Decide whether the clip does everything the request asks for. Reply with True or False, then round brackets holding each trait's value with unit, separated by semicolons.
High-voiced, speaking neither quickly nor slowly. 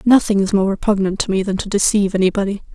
False (200 Hz; 220 wpm)